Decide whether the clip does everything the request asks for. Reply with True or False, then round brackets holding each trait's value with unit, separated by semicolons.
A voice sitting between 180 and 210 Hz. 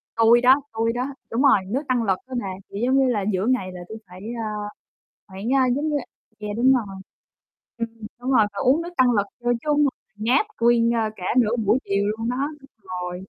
False (230 Hz)